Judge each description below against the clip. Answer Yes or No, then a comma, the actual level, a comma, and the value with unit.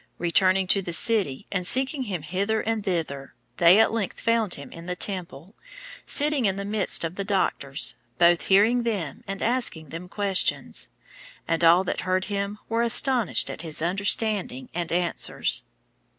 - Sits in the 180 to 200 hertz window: Yes, high, 190 Hz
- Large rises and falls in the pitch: No, average, 4.1 semitones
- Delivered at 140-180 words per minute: Yes, average, 165 wpm